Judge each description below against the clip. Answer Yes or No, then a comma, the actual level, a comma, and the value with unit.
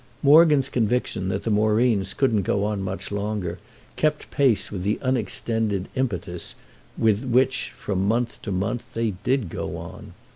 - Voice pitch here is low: Yes, low, 110 Hz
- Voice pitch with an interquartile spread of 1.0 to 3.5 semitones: No, average, 4.2 semitones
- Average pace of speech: Yes, average, 150 wpm